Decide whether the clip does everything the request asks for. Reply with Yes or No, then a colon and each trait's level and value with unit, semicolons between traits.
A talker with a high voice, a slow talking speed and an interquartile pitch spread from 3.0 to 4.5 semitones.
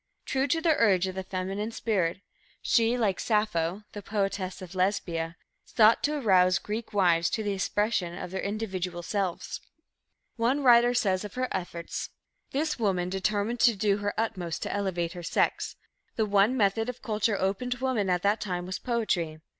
No: high, 200 Hz; average, 180 wpm; average, 3.6 semitones